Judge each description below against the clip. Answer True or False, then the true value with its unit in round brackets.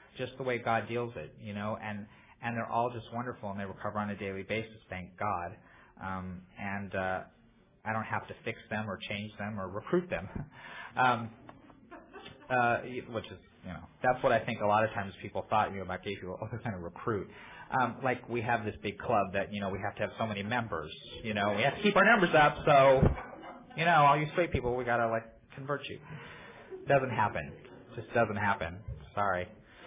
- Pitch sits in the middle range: False (110 Hz)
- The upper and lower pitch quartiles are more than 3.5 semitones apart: False (3.2 semitones)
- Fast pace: True (220 wpm)